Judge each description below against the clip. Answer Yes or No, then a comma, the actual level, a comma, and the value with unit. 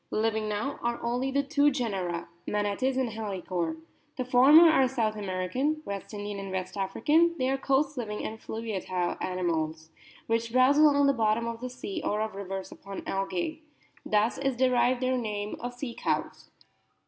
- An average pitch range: Yes, average, 4.8 semitones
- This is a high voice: Yes, high, 225 Hz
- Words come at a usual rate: Yes, average, 170 wpm